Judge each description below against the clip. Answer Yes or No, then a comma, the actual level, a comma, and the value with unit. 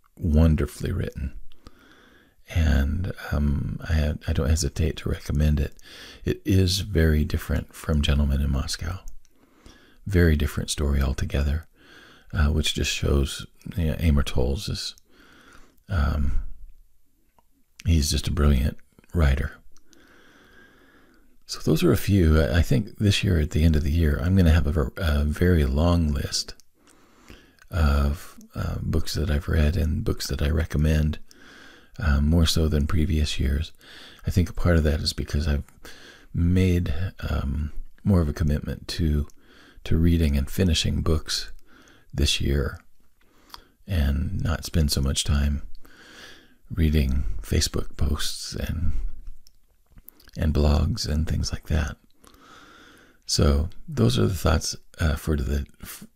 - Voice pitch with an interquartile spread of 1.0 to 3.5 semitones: Yes, average, 2.9 semitones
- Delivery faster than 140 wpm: No, slow, 135 wpm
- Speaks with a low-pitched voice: Yes, very low, 80 Hz